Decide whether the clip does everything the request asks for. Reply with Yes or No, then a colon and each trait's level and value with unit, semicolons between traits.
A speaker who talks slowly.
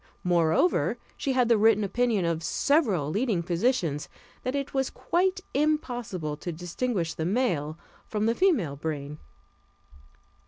Yes: slow, 130 wpm